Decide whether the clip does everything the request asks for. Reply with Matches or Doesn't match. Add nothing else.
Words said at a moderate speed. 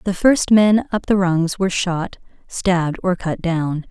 Matches